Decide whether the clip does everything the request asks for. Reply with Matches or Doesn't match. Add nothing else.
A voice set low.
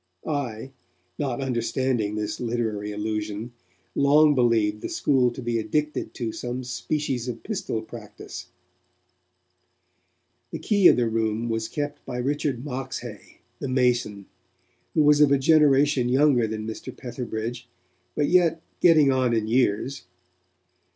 Matches